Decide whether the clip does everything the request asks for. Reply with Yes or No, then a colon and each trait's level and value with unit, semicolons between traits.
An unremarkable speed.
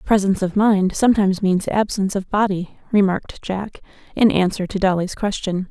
Yes: average, 160 wpm